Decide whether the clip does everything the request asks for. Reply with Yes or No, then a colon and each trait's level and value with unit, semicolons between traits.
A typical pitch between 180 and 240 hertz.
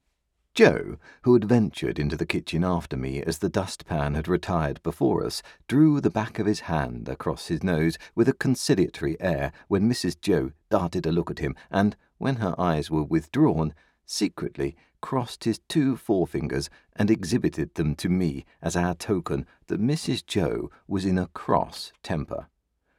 No: very low, 85 Hz